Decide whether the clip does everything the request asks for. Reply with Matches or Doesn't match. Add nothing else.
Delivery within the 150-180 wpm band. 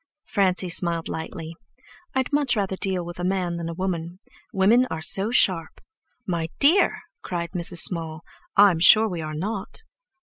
Matches